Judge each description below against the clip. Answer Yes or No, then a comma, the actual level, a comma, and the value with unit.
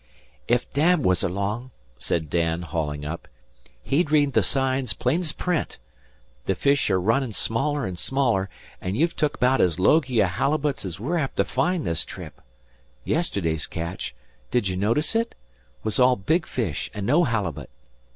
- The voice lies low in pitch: Yes, low, 120 Hz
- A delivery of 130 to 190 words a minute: Yes, average, 160 wpm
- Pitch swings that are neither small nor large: No, wide, 7.8 semitones